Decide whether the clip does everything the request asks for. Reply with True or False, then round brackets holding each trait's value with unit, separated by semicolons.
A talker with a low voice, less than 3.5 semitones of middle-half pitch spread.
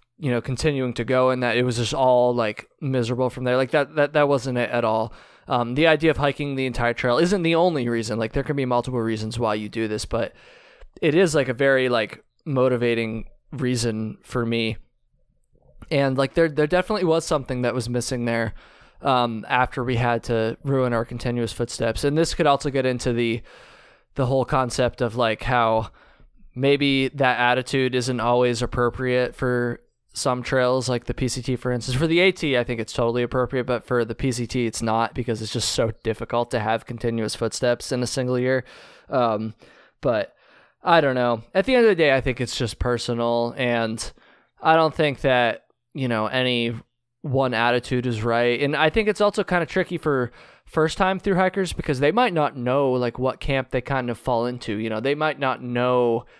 True (125 Hz; 2.6 semitones)